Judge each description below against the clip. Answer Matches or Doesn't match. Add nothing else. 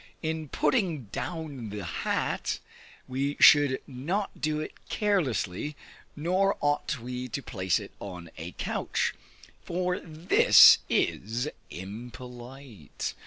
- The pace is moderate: Doesn't match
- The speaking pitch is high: Doesn't match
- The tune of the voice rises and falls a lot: Matches